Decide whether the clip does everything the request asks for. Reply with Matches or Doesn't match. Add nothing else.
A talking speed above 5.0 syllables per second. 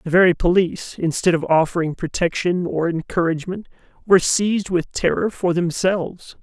Matches